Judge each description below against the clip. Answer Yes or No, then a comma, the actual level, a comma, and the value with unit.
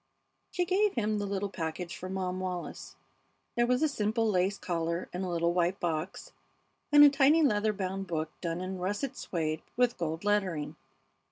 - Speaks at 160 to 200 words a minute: Yes, average, 175 wpm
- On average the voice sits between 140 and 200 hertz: Yes, high, 190 Hz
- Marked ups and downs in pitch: No, average, 4.3 semitones